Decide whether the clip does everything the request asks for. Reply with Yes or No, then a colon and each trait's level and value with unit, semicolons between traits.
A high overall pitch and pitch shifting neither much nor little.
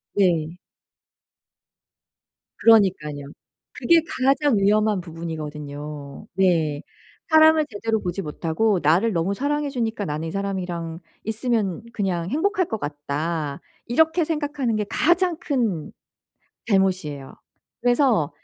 No: high, 195 Hz; wide, 7.2 semitones